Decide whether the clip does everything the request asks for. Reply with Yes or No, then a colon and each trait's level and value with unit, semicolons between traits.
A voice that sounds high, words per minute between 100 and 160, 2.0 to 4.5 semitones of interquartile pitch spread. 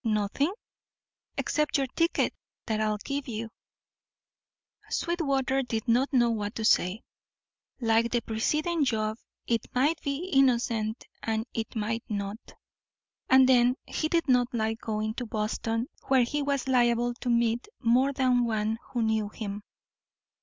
Yes: high, 235 Hz; average, 140 wpm; average, 3.3 semitones